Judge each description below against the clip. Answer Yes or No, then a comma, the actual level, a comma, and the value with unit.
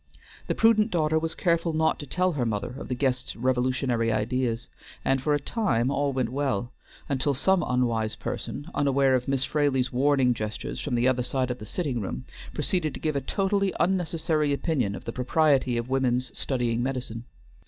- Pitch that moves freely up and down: No, average, 3.7 semitones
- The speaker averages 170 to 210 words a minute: Yes, average, 185 wpm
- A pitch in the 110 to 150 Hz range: Yes, low, 135 Hz